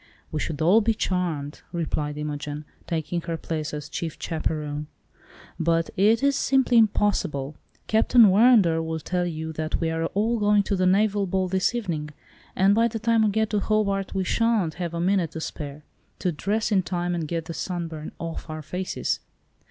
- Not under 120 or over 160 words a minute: No, average, 185 wpm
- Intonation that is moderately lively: Yes, average, 4.5 semitones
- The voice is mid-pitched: Yes, medium, 175 Hz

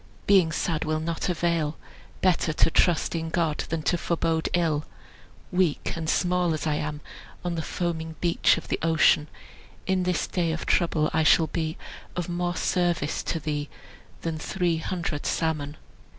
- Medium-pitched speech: Yes, medium, 165 Hz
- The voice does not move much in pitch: Yes, narrow, 1.9 semitones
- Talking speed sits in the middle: Yes, average, 165 wpm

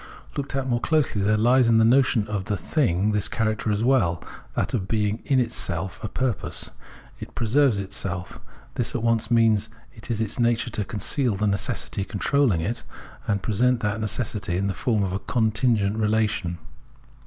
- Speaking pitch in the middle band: No, low, 110 Hz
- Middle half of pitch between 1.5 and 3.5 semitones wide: Yes, average, 3.0 semitones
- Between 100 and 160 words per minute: No, average, 185 wpm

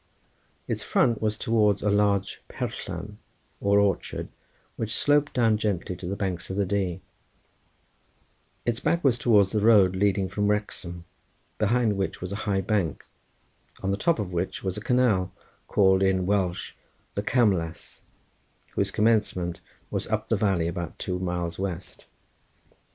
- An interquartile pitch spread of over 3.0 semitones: No, narrow, 2.6 semitones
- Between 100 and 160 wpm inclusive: Yes, average, 150 wpm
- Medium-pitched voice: No, low, 100 Hz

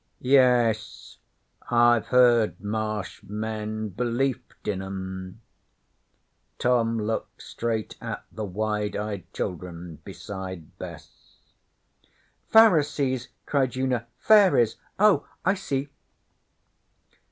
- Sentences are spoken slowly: Yes, slow, 85 wpm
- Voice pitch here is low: Yes, low, 110 Hz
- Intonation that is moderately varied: Yes, average, 4.2 semitones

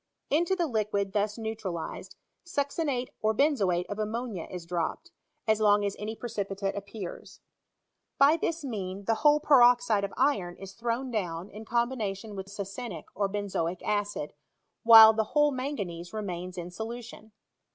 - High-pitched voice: Yes, high, 215 Hz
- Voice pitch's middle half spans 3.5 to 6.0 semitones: Yes, average, 3.8 semitones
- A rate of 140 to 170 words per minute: Yes, average, 145 wpm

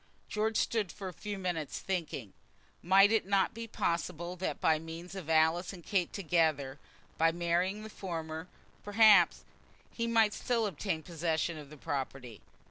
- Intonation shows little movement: No, average, 3.9 semitones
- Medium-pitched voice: Yes, medium, 175 Hz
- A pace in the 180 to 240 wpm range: No, average, 155 wpm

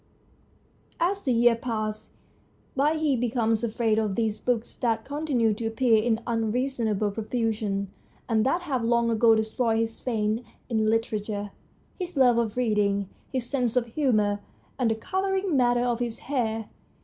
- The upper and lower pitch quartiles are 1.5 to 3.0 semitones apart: Yes, narrow, 2.4 semitones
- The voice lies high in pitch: Yes, high, 230 Hz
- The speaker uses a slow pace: No, average, 150 wpm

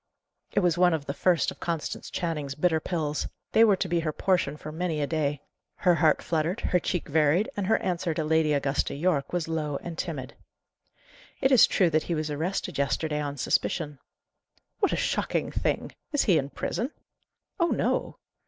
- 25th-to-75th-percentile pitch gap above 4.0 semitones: No, average, 3.2 semitones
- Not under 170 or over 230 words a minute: Yes, average, 190 wpm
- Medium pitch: Yes, medium, 160 Hz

